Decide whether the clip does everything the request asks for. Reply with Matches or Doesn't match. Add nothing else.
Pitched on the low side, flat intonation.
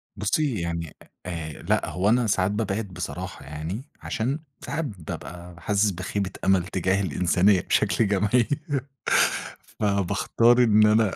Doesn't match